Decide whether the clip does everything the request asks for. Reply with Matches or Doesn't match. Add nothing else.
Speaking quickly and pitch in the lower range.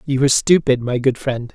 Matches